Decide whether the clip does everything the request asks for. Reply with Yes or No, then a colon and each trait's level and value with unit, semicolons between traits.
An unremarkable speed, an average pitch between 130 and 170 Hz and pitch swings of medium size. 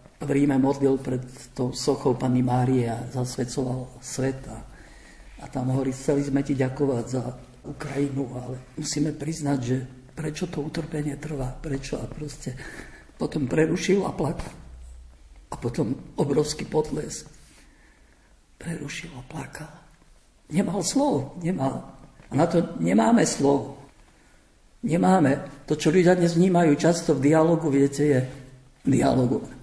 Yes: average, 125 wpm; medium, 140 Hz; average, 3.1 semitones